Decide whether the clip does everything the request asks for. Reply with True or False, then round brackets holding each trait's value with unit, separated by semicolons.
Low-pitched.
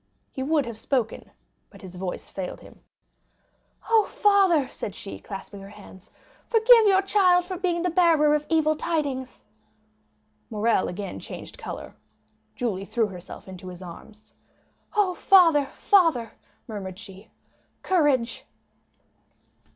False (265 Hz)